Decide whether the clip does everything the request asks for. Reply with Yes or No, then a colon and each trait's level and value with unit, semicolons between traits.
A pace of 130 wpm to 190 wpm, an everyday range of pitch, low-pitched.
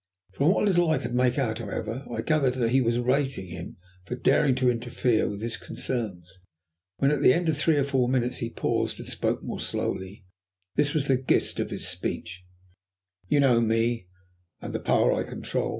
No: average, 200 wpm; average, 3.5 semitones; low, 125 Hz